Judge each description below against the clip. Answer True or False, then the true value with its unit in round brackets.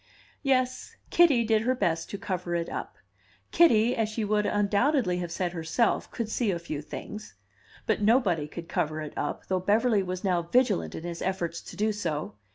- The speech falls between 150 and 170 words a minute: False (185 wpm)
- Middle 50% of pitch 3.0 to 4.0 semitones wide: False (4.9 semitones)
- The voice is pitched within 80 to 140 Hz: False (200 Hz)